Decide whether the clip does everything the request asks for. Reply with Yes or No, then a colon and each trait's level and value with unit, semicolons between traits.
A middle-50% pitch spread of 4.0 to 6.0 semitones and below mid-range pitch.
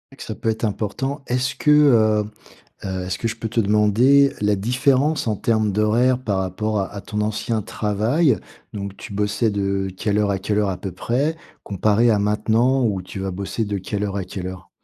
No: average, 3.2 semitones; low, 105 Hz